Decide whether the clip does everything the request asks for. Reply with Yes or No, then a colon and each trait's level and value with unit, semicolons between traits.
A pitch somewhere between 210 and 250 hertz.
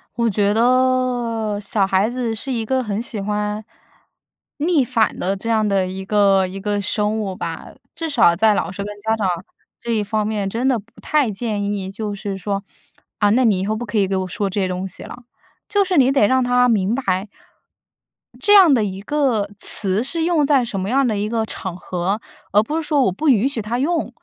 Yes: high, 215 Hz